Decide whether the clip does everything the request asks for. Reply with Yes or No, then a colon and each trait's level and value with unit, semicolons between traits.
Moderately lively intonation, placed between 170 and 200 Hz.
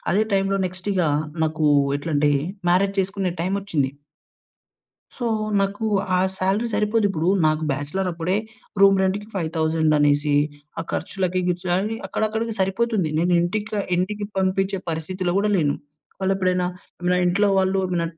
Yes: average, 3.0 semitones; medium, 185 Hz